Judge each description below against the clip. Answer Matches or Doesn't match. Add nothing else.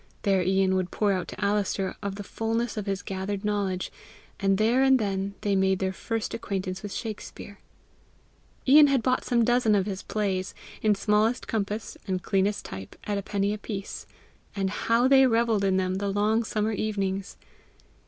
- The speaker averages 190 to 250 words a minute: Doesn't match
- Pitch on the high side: Matches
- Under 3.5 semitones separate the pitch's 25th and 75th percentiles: Matches